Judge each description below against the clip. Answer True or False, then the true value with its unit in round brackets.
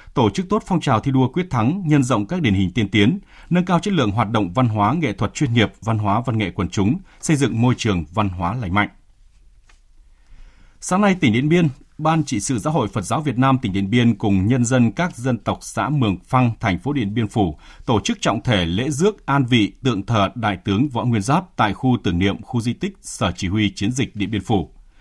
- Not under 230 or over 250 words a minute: True (245 wpm)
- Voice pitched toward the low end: True (120 Hz)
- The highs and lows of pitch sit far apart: True (6.0 semitones)